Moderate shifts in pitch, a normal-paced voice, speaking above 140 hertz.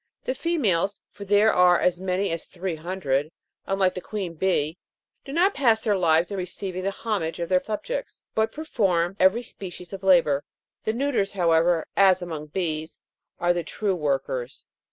Yes: average, 3.5 semitones; average, 170 wpm; medium, 185 Hz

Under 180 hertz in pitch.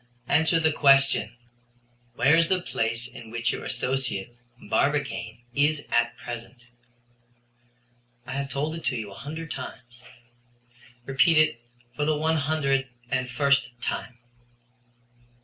Yes: low, 135 Hz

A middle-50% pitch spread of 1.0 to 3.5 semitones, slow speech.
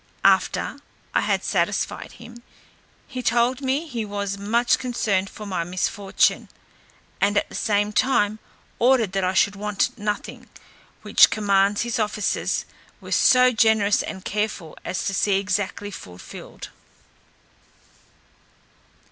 Yes: average, 2.9 semitones; slow, 125 wpm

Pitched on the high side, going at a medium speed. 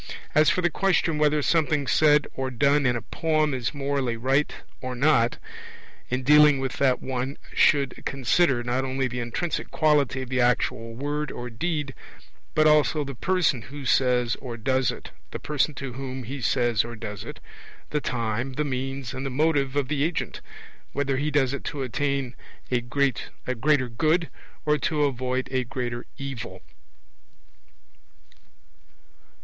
No: low, 135 Hz; average, 160 wpm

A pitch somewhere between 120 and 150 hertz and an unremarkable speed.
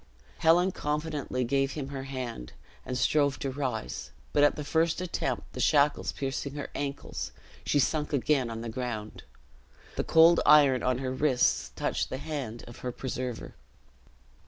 Yes: low, 135 Hz; average, 155 wpm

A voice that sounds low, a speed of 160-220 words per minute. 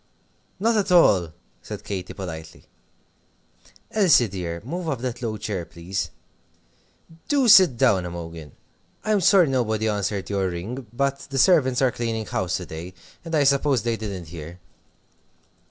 No: low, 110 Hz; average, 145 wpm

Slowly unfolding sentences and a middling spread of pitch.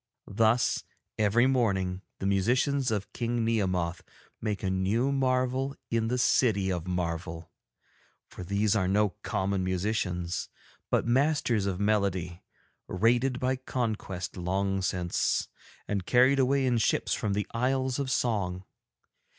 Yes: slow, 130 wpm; average, 5.0 semitones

